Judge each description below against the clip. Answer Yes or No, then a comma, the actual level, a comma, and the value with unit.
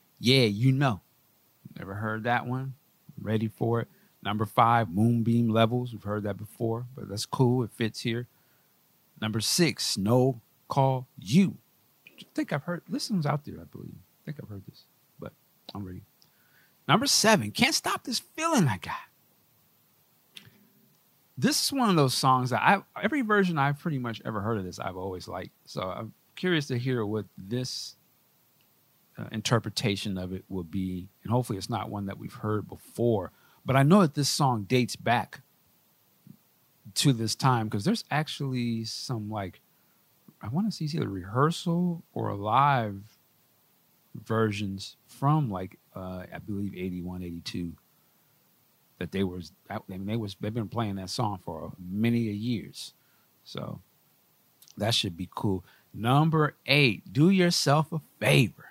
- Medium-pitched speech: No, low, 115 Hz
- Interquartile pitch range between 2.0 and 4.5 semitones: No, wide, 5.5 semitones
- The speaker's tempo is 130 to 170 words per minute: Yes, average, 160 wpm